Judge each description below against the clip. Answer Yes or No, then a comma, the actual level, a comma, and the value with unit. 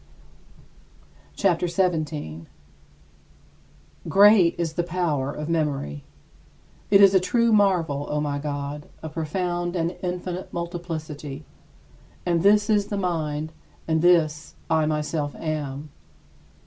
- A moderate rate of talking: No, slow, 115 wpm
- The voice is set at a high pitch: No, medium, 165 Hz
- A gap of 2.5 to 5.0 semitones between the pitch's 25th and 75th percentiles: Yes, average, 3.2 semitones